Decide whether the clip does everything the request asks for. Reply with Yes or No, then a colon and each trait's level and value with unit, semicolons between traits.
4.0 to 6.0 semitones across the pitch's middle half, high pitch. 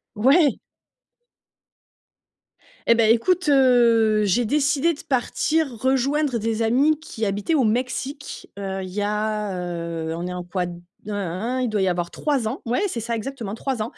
Yes: average, 4.8 semitones; high, 230 Hz